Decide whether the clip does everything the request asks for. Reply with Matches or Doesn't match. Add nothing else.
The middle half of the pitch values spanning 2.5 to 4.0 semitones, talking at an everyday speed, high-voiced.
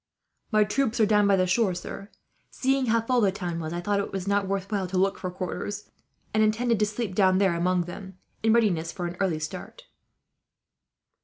Doesn't match